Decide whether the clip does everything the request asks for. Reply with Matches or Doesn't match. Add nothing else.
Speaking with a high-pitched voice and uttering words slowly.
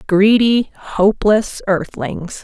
Matches